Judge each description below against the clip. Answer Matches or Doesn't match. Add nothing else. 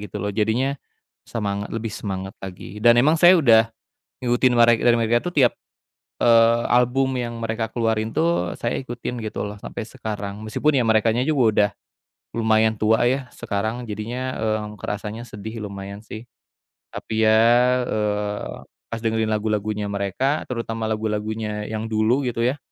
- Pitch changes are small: Matches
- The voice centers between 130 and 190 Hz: Doesn't match